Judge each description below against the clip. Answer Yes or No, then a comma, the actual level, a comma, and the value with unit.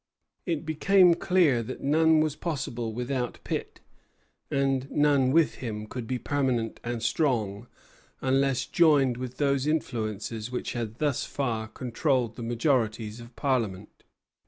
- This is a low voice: Yes, low, 130 Hz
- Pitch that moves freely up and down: No, average, 3.8 semitones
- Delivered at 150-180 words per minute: No, slow, 135 wpm